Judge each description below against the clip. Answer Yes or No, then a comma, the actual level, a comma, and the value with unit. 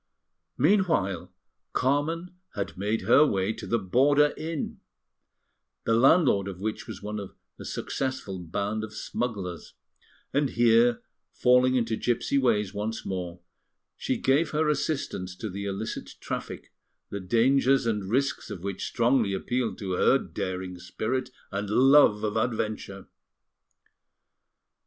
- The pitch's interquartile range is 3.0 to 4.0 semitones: No, average, 5.1 semitones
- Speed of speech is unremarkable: No, slow, 130 wpm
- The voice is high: No, low, 110 Hz